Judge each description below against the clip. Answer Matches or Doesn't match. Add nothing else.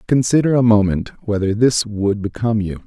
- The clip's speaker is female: Doesn't match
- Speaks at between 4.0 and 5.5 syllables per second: Matches